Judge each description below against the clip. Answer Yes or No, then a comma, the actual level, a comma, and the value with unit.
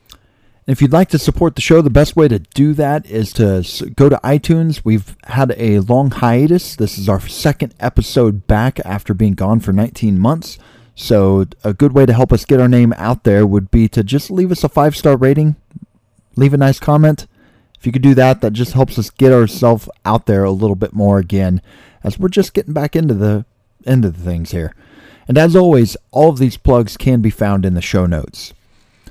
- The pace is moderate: No, fast, 215 wpm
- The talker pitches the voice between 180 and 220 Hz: No, low, 120 Hz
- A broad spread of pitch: Yes, wide, 5.7 semitones